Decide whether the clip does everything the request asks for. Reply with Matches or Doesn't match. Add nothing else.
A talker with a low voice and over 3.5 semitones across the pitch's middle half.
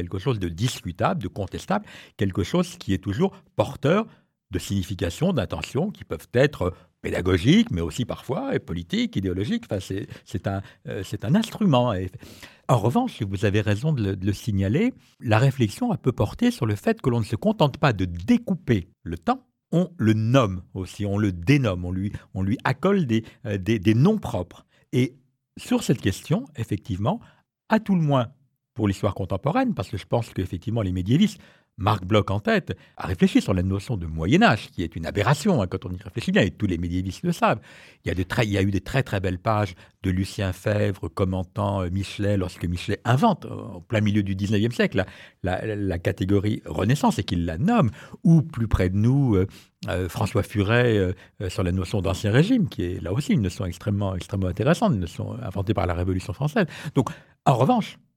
Matches